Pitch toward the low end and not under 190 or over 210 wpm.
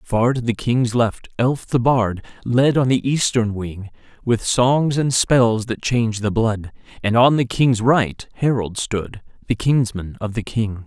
No: low, 115 Hz; average, 180 wpm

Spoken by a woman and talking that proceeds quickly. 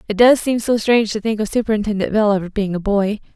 Yes: female; fast, 250 wpm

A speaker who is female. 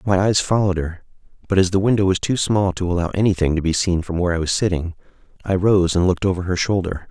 No: male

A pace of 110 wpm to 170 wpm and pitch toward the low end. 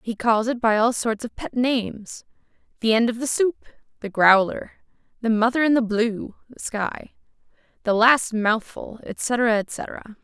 No: average, 165 wpm; high, 230 Hz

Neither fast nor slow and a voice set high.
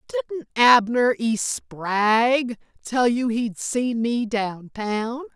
No: slow, 125 wpm; high, 235 Hz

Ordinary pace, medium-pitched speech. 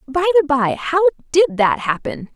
No: average, 180 wpm; very high, 295 Hz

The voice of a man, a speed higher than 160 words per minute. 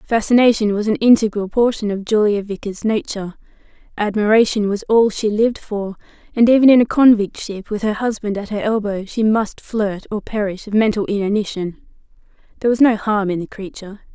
No: female; average, 180 wpm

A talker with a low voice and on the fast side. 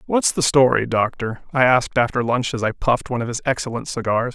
Yes: low, 125 Hz; fast, 220 wpm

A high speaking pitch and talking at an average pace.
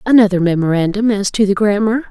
Yes: high, 205 Hz; average, 170 wpm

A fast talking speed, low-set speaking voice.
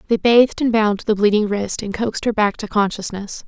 No: fast, 225 wpm; high, 215 Hz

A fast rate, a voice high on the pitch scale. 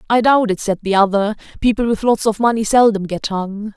Yes: fast, 225 wpm; high, 215 Hz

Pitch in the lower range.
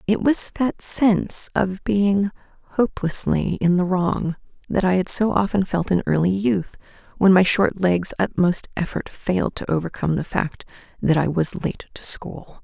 No: medium, 185 Hz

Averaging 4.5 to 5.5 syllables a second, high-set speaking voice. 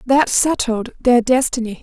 No: 4.3 syllables/s; high, 245 Hz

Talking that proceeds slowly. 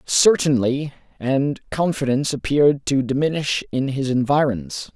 Yes: slow, 110 wpm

